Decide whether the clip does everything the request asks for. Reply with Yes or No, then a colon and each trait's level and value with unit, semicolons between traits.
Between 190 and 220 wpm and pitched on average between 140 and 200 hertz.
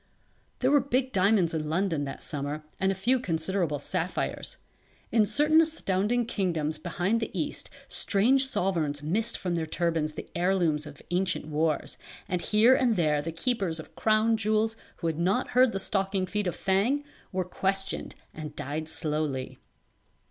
No: average, 160 wpm; medium, 185 Hz